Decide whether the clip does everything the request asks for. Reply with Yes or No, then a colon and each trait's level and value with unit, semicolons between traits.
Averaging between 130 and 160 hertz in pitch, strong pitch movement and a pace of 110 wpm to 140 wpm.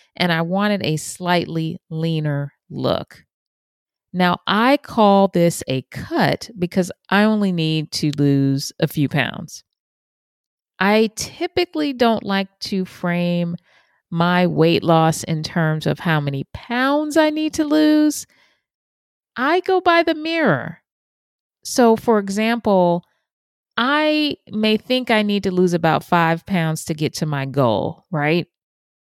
No: medium, 180 Hz; wide, 5.8 semitones; slow, 135 wpm